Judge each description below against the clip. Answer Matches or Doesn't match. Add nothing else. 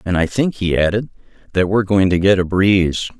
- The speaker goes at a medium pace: Doesn't match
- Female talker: Doesn't match